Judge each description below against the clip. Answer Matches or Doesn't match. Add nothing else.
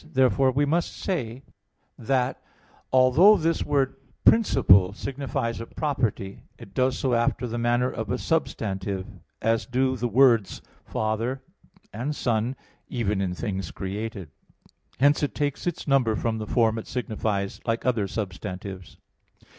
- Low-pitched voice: Matches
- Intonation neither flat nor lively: Matches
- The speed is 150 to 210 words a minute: Doesn't match